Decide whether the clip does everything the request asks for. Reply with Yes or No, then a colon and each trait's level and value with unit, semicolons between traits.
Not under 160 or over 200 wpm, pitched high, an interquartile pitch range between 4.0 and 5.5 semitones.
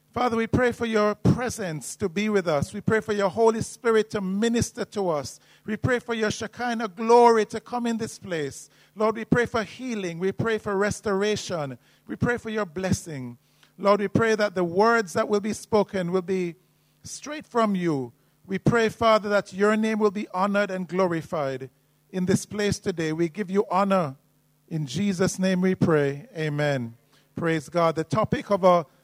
Yes: average, 190 wpm; high, 200 Hz; average, 4.5 semitones